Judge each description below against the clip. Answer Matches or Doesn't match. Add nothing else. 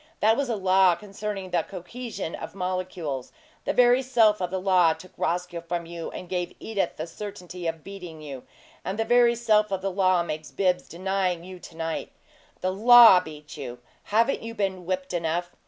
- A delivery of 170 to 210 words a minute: Matches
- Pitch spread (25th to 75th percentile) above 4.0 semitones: Doesn't match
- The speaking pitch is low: Doesn't match